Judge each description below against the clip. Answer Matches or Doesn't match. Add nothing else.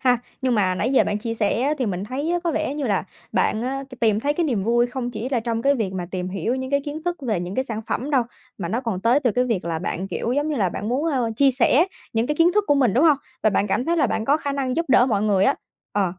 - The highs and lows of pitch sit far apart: Doesn't match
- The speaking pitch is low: Doesn't match